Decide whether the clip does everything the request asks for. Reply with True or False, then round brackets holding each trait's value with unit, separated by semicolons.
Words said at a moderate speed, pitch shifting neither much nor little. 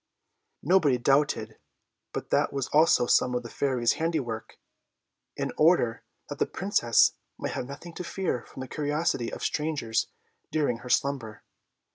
True (145 wpm; 4.7 semitones)